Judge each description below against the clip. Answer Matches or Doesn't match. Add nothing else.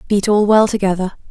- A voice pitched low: Doesn't match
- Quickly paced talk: Doesn't match